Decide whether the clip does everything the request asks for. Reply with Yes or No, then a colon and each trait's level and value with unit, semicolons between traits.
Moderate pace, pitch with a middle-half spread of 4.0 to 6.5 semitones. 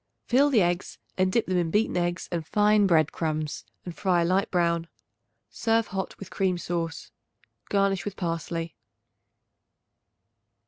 No: average, 145 wpm; average, 2.8 semitones